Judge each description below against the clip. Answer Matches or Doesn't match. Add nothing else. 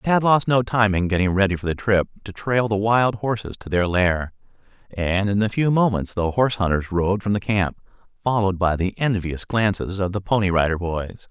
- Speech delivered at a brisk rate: Matches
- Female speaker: Doesn't match